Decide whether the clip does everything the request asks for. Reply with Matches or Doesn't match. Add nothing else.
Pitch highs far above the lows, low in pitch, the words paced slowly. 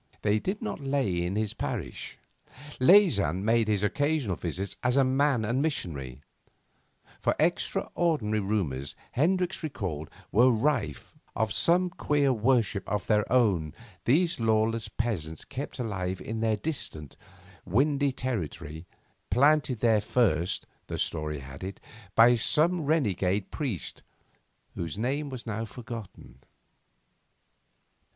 Matches